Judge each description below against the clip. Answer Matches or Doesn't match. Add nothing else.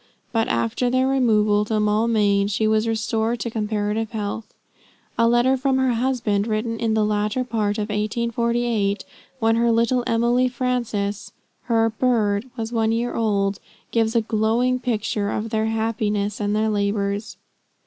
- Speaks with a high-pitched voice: Matches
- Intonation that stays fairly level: Matches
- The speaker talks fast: Doesn't match